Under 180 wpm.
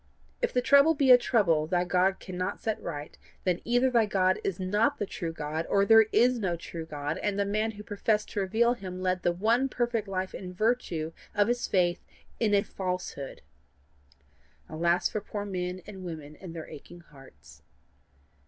No: average, 185 wpm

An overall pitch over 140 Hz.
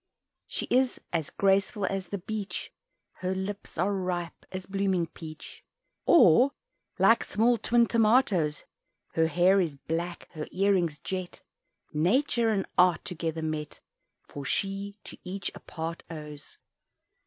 Yes: medium, 185 Hz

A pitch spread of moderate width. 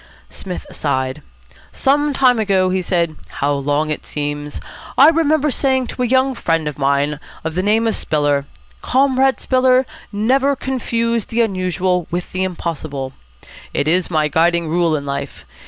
No: wide, 9.0 semitones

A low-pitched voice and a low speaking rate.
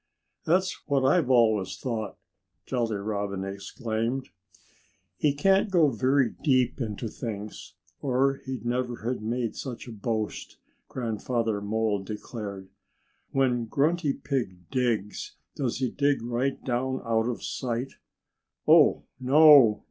Yes: low, 120 Hz; slow, 120 wpm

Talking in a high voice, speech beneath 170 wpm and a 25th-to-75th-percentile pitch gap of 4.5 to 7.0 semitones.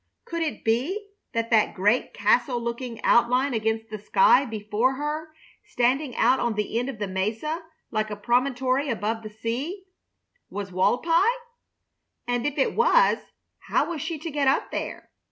Yes: high, 245 Hz; average, 160 wpm; average, 4.8 semitones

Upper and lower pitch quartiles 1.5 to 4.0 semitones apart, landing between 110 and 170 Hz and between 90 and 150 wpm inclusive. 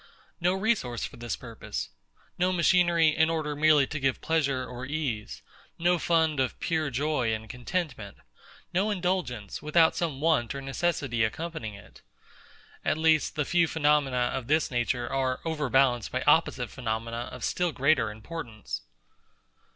No: average, 5.1 semitones; medium, 140 Hz; average, 145 wpm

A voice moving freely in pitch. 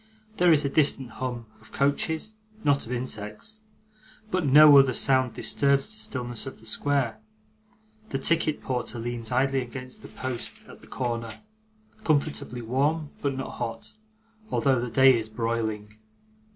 No: average, 3.3 semitones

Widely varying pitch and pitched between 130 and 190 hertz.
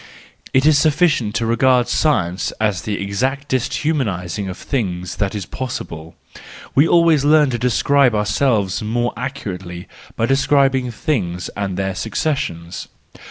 No: wide, 6.2 semitones; low, 120 Hz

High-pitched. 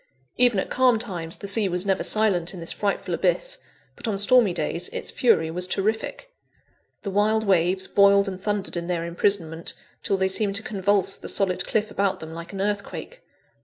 Yes: high, 195 Hz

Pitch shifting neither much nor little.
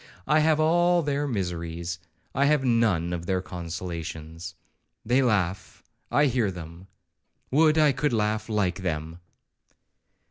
No: wide, 8.4 semitones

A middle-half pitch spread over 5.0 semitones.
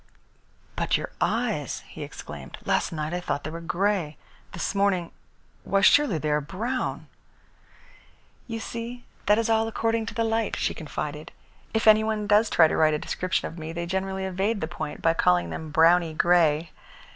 Yes: wide, 5.6 semitones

